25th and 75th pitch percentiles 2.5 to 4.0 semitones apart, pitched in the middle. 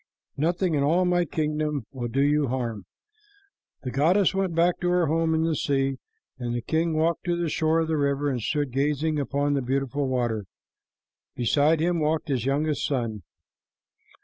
Yes: average, 3.3 semitones; medium, 150 Hz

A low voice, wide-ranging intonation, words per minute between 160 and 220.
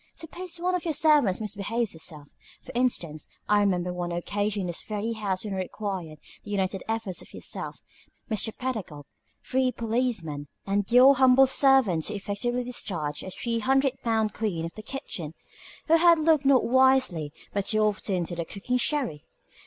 No: high, 215 Hz; wide, 5.8 semitones; average, 170 wpm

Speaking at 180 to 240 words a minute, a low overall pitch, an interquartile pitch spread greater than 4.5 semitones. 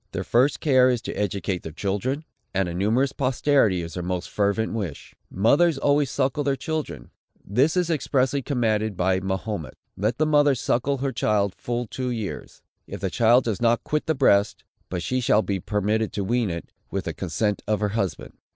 Yes: average, 190 wpm; low, 110 Hz; average, 5.2 semitones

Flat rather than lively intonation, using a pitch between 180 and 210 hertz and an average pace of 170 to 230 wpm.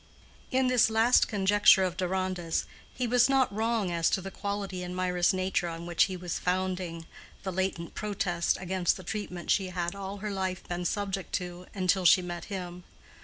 Yes: narrow, 2.2 semitones; medium, 185 Hz; average, 175 wpm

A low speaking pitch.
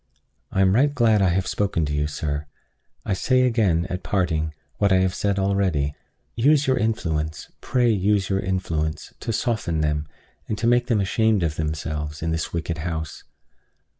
Yes: very low, 95 Hz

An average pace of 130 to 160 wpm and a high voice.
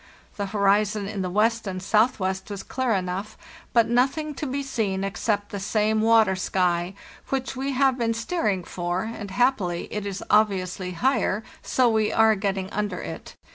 No: average, 175 wpm; high, 210 Hz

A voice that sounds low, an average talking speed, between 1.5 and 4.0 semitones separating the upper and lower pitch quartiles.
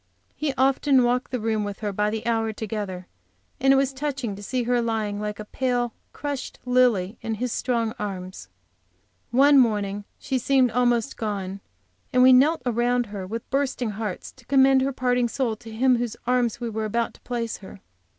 No: high, 235 Hz; average, 190 wpm; average, 3.2 semitones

